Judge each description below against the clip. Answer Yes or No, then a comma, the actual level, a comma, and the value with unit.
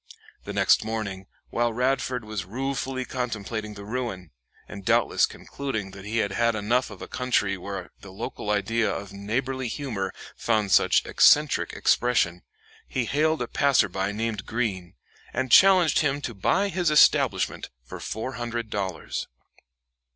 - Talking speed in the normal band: Yes, average, 150 wpm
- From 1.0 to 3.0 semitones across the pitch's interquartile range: No, average, 4.2 semitones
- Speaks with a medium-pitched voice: No, low, 115 Hz